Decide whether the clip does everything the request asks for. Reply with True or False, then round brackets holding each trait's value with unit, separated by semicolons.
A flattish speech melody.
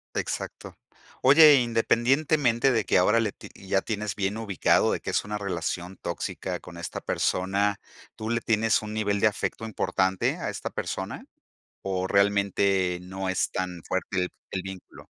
False (3.2 semitones)